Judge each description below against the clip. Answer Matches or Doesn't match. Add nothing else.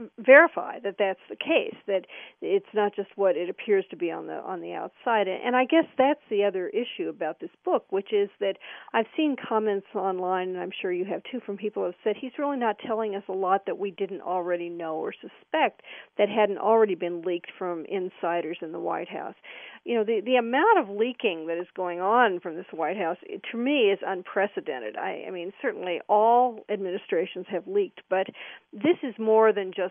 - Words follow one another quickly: Matches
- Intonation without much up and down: Doesn't match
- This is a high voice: Matches